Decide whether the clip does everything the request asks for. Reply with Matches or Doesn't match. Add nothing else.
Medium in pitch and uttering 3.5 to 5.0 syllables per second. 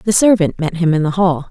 Doesn't match